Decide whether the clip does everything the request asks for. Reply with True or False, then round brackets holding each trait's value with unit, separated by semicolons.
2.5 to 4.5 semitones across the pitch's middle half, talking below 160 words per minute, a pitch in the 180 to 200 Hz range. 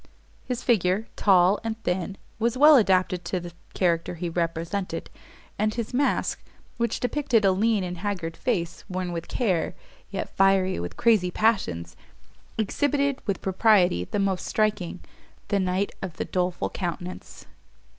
True (3.7 semitones; 145 wpm; 190 Hz)